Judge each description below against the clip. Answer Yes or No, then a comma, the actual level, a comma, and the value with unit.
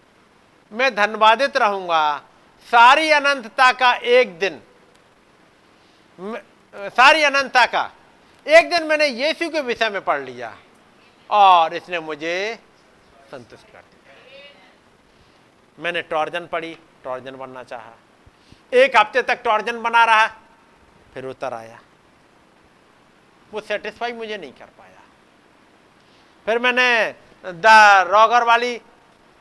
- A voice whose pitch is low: No, high, 220 Hz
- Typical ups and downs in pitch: No, wide, 6.3 semitones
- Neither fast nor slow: No, slow, 105 wpm